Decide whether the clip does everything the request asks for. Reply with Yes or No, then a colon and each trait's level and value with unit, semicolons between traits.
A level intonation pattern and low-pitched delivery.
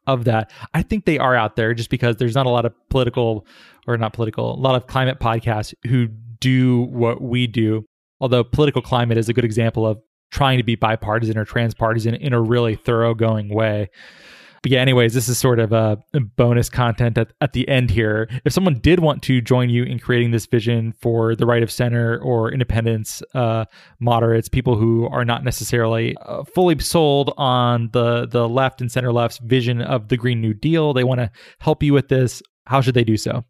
Yes: narrow, 2.1 semitones; low, 120 Hz